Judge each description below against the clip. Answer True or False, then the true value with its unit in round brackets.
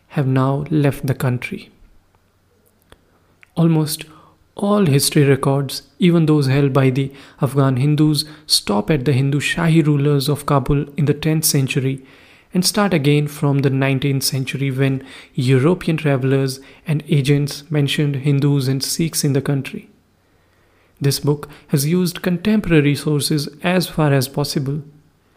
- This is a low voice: False (145 Hz)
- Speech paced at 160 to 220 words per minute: False (135 wpm)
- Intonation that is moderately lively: False (2.2 semitones)